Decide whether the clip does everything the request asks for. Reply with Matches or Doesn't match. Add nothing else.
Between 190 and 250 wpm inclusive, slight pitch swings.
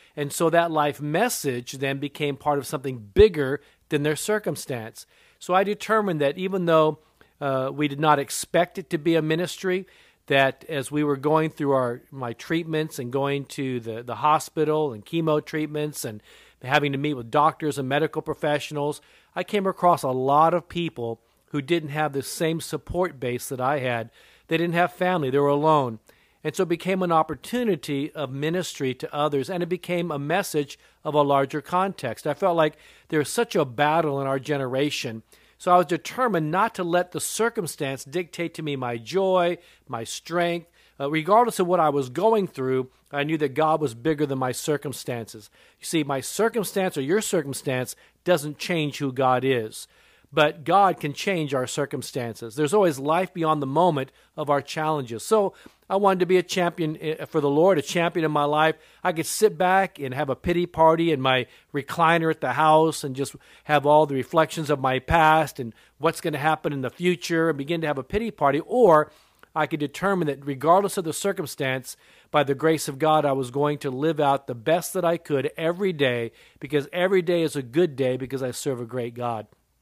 Doesn't match